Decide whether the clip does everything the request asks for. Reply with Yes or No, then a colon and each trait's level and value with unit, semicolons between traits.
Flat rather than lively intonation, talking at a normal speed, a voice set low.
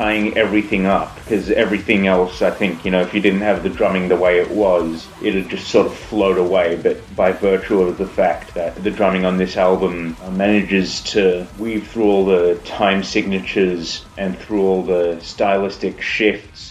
Yes: narrow, 2.2 semitones; average, 185 wpm; very low, 95 Hz